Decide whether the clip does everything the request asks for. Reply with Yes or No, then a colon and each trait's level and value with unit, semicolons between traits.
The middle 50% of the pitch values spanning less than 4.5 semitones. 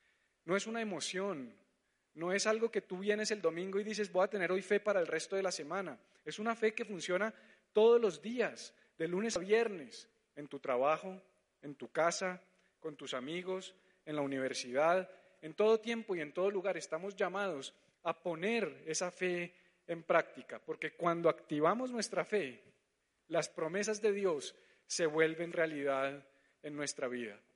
No: average, 4.8 semitones